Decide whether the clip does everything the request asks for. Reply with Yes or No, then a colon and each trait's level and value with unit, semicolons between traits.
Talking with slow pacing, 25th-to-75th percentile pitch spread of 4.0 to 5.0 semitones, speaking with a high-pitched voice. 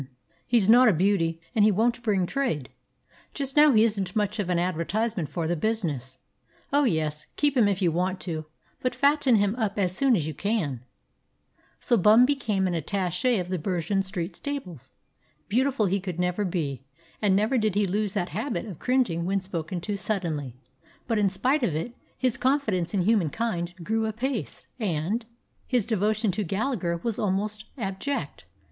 No: average, 175 wpm; average, 4.6 semitones; high, 200 Hz